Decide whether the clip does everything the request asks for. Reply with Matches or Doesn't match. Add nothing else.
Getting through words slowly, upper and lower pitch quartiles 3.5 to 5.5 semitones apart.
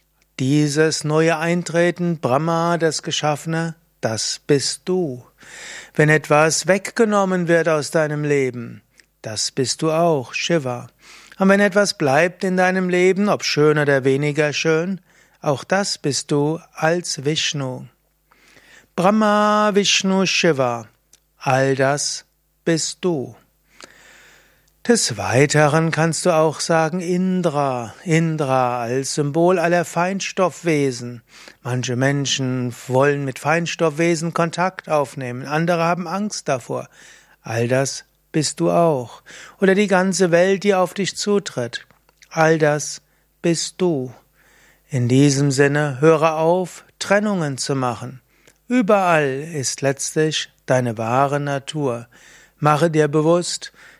Matches